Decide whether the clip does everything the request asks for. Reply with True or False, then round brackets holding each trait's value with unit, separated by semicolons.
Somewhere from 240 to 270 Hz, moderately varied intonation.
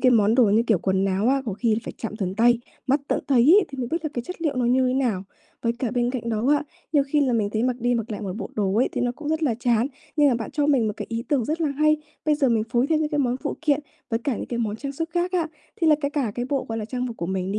True (245 Hz; 4.3 semitones)